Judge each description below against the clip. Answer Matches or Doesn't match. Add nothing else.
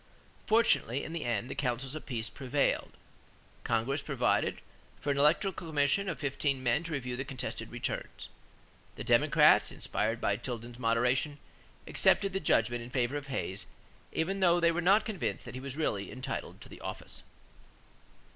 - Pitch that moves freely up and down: Doesn't match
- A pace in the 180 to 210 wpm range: Doesn't match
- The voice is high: Doesn't match